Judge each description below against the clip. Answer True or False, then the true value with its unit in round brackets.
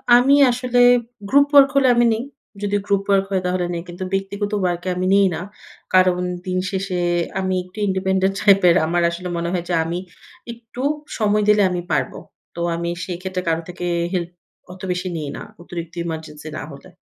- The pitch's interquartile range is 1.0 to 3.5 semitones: True (2.5 semitones)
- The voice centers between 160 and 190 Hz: True (185 Hz)